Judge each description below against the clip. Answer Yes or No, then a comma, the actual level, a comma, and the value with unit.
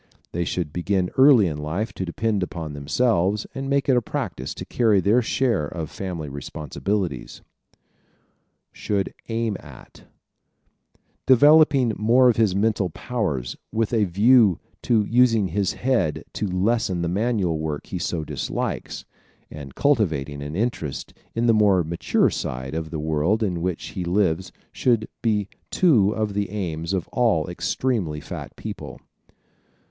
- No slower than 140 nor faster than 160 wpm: Yes, average, 150 wpm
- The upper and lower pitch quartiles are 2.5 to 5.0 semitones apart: No, wide, 5.6 semitones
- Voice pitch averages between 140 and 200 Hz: No, low, 100 Hz